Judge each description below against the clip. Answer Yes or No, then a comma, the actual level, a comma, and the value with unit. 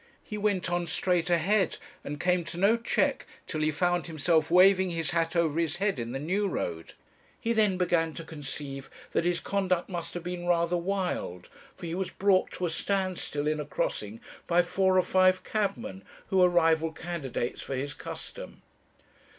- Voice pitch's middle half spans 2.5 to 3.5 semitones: Yes, average, 2.8 semitones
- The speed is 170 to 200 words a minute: Yes, average, 185 wpm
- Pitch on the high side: No, medium, 175 Hz